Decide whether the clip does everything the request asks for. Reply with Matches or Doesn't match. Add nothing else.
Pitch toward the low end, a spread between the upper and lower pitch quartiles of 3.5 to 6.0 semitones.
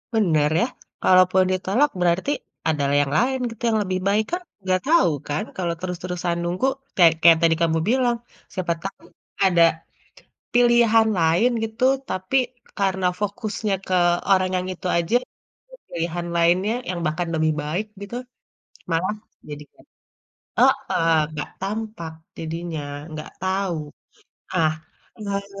Doesn't match